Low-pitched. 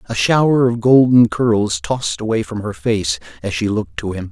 Yes: low, 105 Hz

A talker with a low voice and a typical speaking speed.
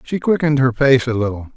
No: low, 130 Hz; fast, 230 wpm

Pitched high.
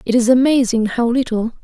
Yes: high, 240 Hz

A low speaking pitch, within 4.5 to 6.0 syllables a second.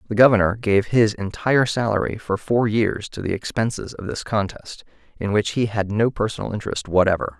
Yes: low, 105 Hz; 5.5 syllables/s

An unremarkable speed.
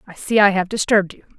No: fast, 260 wpm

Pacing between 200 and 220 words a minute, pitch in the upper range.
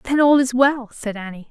No: fast, 240 wpm; high, 245 Hz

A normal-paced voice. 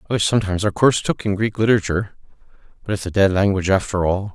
No: fast, 220 wpm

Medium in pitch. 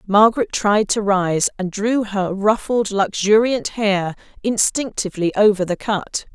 No: high, 205 Hz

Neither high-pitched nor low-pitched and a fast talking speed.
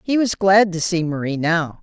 Yes: medium, 180 Hz; fast, 230 wpm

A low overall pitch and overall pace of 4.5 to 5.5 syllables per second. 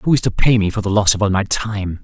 No: low, 105 Hz; 6.0 syllables/s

